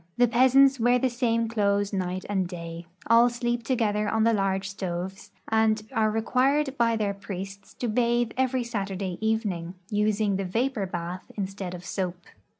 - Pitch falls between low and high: No, high, 215 Hz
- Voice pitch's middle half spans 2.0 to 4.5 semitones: Yes, average, 3.7 semitones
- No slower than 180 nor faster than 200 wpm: No, average, 160 wpm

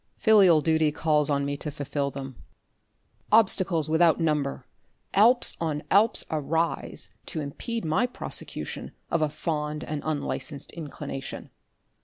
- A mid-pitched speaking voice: Yes, medium, 155 Hz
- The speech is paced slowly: Yes, slow, 125 wpm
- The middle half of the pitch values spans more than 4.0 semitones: No, average, 2.7 semitones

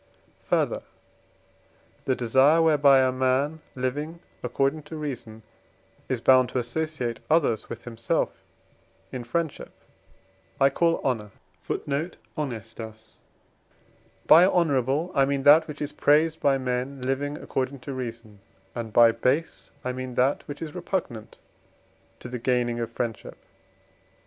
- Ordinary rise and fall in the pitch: Yes, average, 3.6 semitones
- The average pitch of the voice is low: Yes, low, 130 Hz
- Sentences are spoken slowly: Yes, slow, 125 wpm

